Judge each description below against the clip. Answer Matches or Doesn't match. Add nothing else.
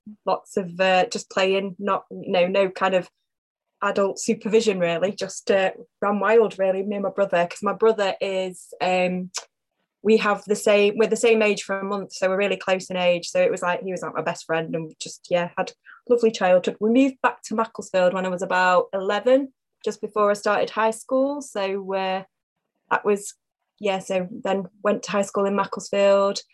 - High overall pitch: Matches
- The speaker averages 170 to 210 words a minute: Matches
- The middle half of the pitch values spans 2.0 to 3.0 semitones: Matches